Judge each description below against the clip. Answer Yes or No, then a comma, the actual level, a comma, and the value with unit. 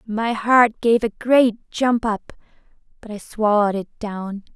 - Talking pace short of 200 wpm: Yes, average, 160 wpm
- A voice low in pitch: No, high, 220 Hz